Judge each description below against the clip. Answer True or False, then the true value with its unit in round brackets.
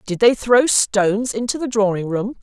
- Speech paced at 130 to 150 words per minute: False (200 wpm)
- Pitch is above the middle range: True (220 Hz)